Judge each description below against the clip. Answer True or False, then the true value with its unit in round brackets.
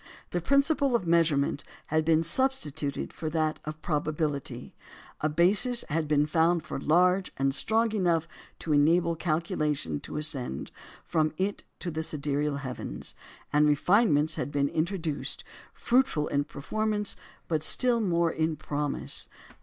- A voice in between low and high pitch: True (160 Hz)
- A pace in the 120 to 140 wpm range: True (135 wpm)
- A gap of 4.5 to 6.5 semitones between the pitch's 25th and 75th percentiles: False (3.4 semitones)